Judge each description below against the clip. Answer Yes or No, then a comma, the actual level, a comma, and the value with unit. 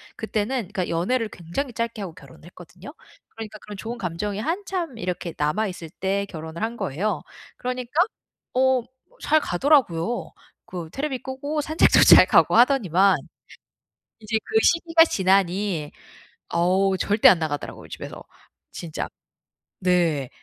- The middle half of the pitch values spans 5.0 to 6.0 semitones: No, wide, 6.4 semitones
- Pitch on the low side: No, high, 205 Hz